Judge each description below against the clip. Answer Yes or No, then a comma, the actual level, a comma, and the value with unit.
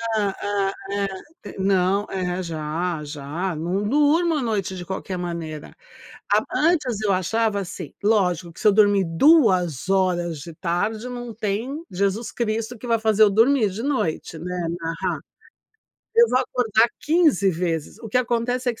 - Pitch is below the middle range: No, high, 200 Hz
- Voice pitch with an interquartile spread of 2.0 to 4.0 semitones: No, average, 4.7 semitones